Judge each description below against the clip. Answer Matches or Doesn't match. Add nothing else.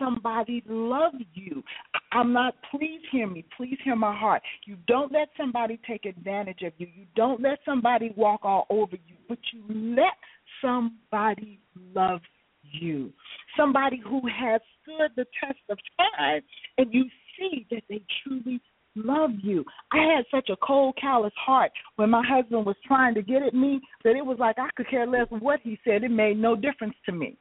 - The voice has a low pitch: Doesn't match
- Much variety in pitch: Doesn't match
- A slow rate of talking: Doesn't match